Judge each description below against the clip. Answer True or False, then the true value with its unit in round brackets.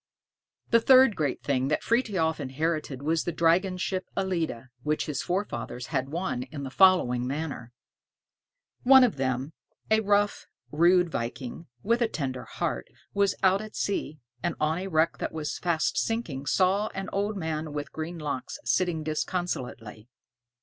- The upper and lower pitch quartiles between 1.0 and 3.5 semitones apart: False (5.3 semitones)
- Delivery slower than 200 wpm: True (155 wpm)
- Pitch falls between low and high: True (160 Hz)